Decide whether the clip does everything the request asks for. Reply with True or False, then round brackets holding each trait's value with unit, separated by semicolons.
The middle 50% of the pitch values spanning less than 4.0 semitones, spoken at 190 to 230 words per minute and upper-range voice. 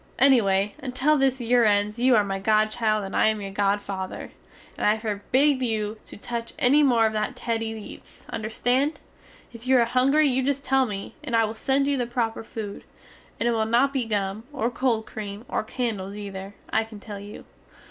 True (3.4 semitones; 200 wpm; 225 Hz)